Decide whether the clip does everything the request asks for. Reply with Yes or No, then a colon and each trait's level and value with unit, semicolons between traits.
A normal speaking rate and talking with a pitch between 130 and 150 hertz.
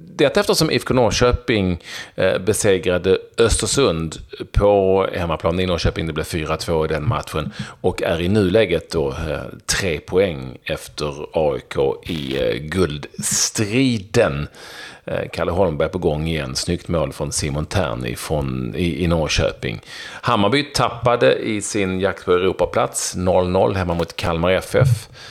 No: average, 135 wpm; very low, 95 Hz